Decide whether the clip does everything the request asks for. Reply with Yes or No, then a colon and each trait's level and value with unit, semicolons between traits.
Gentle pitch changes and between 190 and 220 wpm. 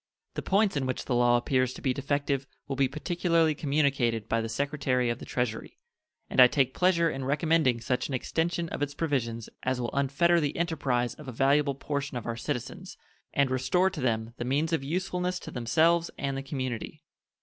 No: average, 4.2 semitones; average, 195 wpm